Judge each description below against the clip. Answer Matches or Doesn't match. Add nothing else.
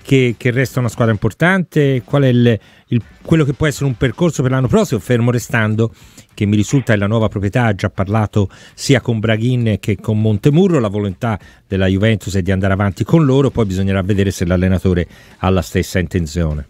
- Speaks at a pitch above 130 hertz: Doesn't match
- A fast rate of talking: Matches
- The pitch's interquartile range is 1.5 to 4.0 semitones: Doesn't match